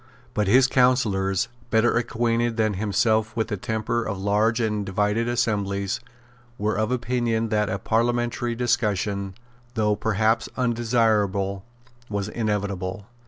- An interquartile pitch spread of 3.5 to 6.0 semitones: No, narrow, 2.6 semitones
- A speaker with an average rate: No, slow, 120 wpm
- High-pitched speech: No, low, 110 Hz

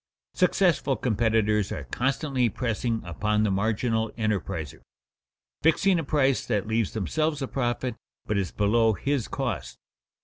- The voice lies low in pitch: Yes, low, 115 Hz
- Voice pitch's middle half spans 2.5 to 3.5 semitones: No, average, 4.1 semitones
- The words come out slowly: Yes, slow, 130 wpm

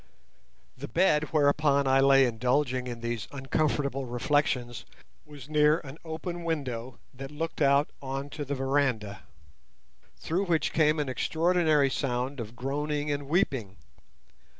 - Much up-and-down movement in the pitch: No, average, 2.8 semitones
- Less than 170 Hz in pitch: Yes, medium, 140 Hz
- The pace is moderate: No, slow, 125 wpm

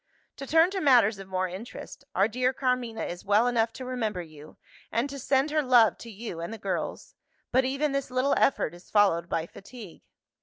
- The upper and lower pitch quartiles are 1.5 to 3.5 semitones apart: No, average, 5.2 semitones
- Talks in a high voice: Yes, high, 230 Hz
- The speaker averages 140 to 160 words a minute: No, average, 200 wpm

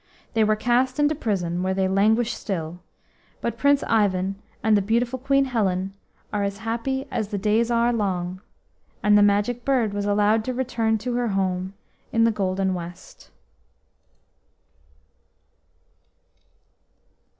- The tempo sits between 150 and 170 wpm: No, average, 140 wpm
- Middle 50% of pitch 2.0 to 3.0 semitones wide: No, average, 3.6 semitones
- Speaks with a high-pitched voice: Yes, high, 215 Hz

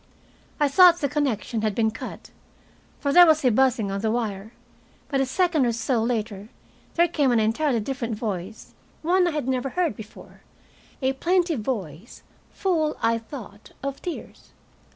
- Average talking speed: Yes, average, 165 wpm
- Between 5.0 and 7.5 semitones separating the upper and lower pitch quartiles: Yes, wide, 5.5 semitones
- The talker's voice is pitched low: No, very high, 255 Hz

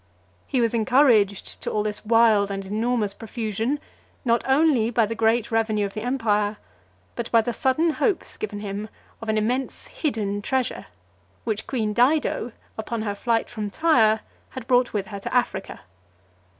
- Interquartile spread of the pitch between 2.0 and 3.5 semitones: Yes, average, 2.8 semitones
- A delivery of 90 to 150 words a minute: No, average, 165 wpm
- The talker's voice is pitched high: Yes, high, 225 Hz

